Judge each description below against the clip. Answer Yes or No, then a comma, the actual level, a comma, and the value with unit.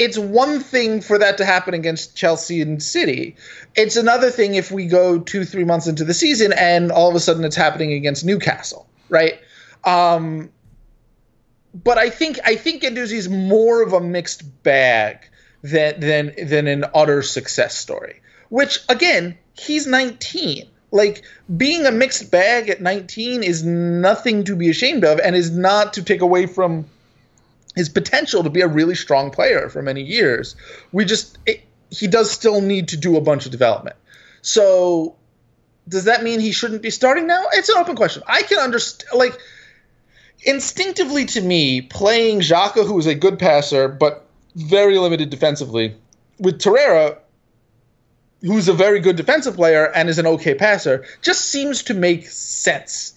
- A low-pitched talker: No, medium, 185 Hz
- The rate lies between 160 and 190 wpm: Yes, average, 170 wpm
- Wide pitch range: Yes, wide, 6.3 semitones